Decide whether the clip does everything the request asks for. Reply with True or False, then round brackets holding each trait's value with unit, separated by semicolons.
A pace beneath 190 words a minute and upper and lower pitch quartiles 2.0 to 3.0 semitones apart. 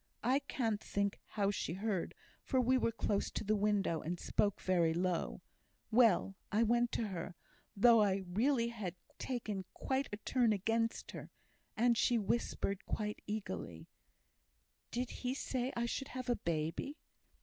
False (155 wpm; 3.6 semitones)